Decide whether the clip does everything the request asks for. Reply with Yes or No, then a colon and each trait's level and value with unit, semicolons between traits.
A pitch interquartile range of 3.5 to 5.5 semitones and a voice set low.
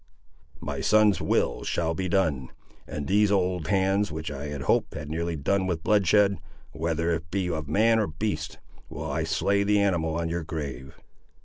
Yes: average, 4.0 semitones; very low, 85 Hz